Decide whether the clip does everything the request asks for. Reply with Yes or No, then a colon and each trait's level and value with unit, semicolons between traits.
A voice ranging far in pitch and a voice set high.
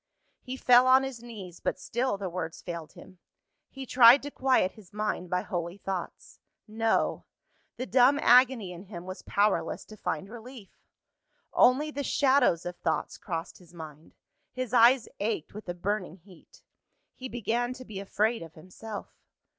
Yes: wide, 5.7 semitones; high, 215 Hz